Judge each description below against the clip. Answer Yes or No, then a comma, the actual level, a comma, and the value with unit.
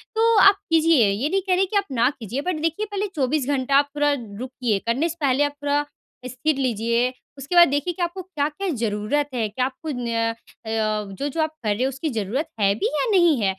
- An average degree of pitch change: No, wide, 5.7 semitones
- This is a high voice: Yes, very high, 275 Hz